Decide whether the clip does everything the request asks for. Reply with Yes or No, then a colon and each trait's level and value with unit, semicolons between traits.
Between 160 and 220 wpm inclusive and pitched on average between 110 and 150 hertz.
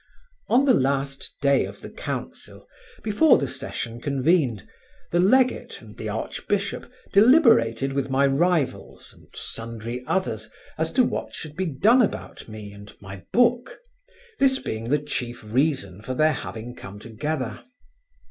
No: average, 145 wpm; medium, 140 Hz